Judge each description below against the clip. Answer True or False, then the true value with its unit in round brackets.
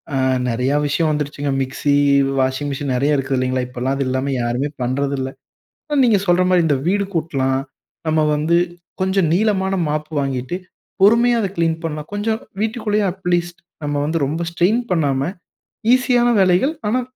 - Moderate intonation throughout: False (5.8 semitones)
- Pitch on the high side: False (155 Hz)